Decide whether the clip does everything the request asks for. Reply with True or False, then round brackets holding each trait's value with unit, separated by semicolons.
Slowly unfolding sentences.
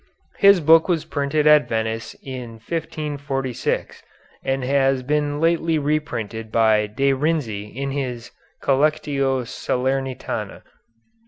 True (105 wpm)